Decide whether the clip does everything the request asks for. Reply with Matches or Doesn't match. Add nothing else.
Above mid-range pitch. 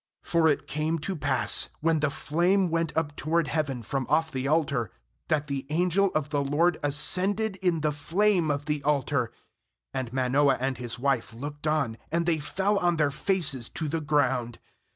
Doesn't match